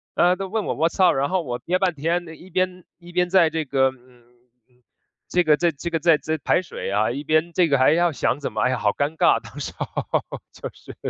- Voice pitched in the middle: Yes, medium, 160 Hz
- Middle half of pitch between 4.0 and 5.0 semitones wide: Yes, average, 4.7 semitones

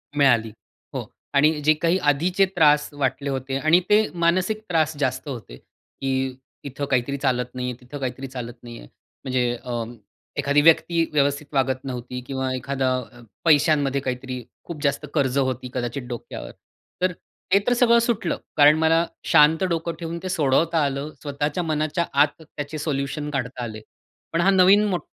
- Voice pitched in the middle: Yes, medium, 145 Hz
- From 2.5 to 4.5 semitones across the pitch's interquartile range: Yes, average, 3.9 semitones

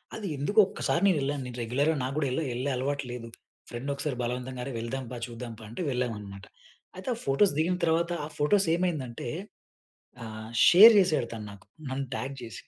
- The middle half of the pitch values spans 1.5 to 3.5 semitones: No, average, 5.0 semitones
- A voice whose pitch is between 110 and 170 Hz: Yes, low, 135 Hz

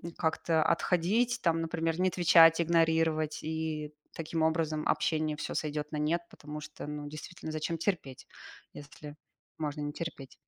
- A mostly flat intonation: Yes, narrow, 1.6 semitones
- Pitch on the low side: No, medium, 160 Hz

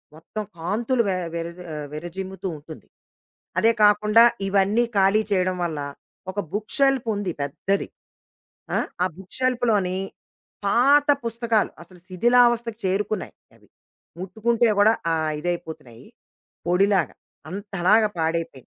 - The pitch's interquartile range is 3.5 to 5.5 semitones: Yes, average, 4.4 semitones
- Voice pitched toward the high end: Yes, high, 200 Hz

